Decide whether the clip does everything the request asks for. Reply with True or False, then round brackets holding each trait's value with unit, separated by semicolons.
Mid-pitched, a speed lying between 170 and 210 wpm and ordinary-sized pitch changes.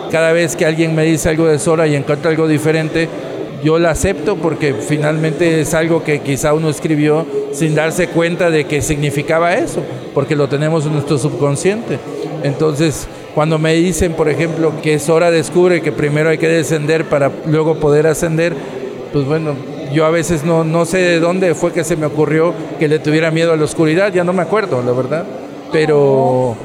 False (160 Hz; 190 wpm; 1.7 semitones)